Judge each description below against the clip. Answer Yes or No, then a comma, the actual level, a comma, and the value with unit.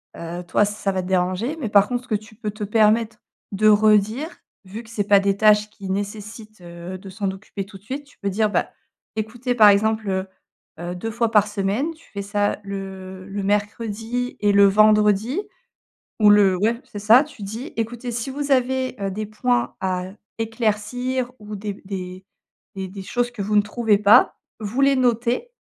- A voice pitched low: No, high, 210 Hz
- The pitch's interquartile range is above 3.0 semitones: No, average, 2.7 semitones